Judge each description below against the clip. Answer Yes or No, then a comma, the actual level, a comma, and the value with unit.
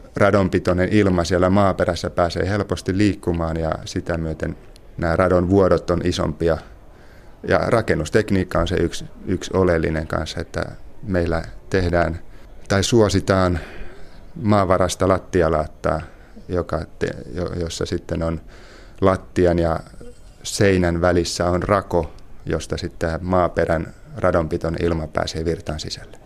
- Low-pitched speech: Yes, very low, 90 Hz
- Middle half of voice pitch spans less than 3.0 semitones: Yes, narrow, 2.5 semitones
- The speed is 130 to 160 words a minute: No, average, 105 wpm